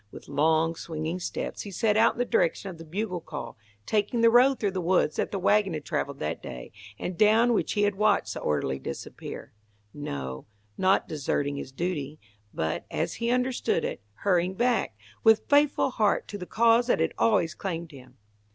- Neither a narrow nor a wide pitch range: No, wide, 6.2 semitones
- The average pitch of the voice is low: No, medium, 185 Hz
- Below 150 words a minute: No, average, 190 wpm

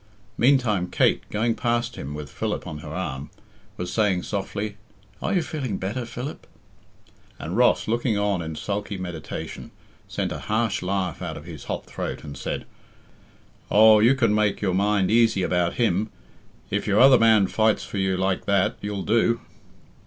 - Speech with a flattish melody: No, average, 3.7 semitones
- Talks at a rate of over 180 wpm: No, average, 165 wpm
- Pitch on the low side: Yes, low, 105 Hz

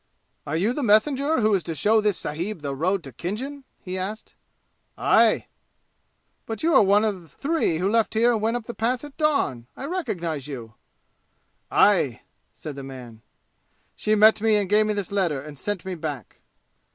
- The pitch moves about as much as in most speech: No, wide, 6.1 semitones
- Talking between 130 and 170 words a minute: No, average, 185 wpm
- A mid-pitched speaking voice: No, high, 205 Hz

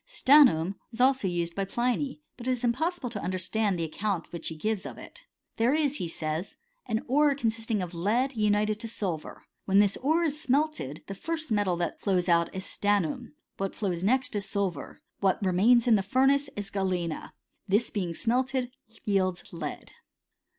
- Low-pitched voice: No, high, 205 Hz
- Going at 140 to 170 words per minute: No, average, 185 wpm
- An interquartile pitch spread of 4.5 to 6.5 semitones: Yes, wide, 5.5 semitones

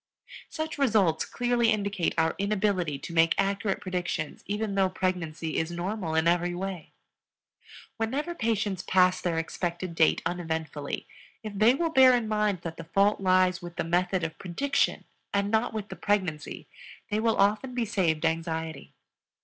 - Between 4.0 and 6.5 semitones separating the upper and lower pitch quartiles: Yes, average, 4.3 semitones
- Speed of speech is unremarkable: Yes, average, 155 wpm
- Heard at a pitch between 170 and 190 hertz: Yes, medium, 185 Hz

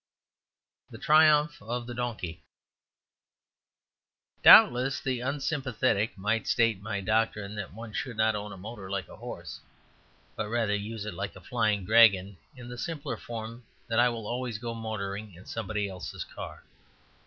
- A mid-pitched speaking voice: No, low, 110 Hz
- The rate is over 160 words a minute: No, average, 155 wpm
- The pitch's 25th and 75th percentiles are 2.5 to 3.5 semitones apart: Yes, average, 3.0 semitones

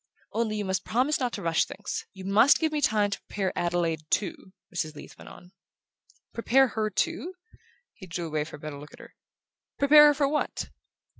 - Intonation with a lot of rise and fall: Yes, wide, 7.7 semitones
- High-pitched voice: Yes, high, 205 Hz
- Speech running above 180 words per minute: Yes, average, 200 wpm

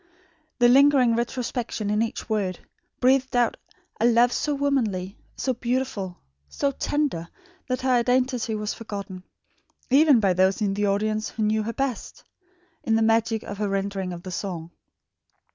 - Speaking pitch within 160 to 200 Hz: No, high, 225 Hz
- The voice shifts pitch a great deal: No, average, 4.1 semitones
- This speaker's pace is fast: No, average, 155 wpm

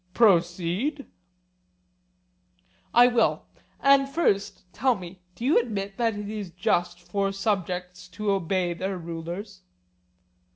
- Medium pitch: No, high, 195 Hz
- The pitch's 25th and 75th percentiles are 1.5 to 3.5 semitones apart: No, average, 3.9 semitones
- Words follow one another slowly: Yes, slow, 115 wpm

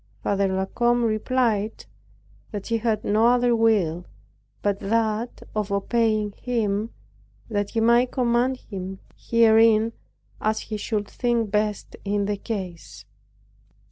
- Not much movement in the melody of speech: Yes, narrow, 2.3 semitones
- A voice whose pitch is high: Yes, high, 215 Hz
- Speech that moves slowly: Yes, slow, 130 wpm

